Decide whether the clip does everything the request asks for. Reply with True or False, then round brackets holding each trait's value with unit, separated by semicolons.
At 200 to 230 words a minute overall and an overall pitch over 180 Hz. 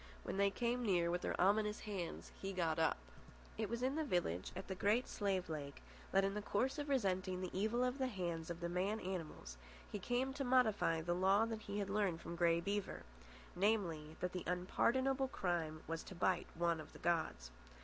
True (205 wpm; 190 Hz)